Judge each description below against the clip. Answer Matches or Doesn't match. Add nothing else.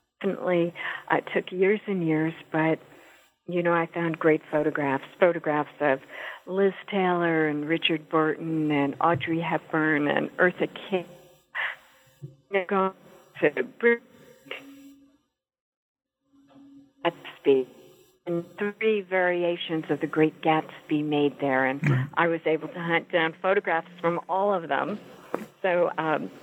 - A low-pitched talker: Doesn't match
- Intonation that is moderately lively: Matches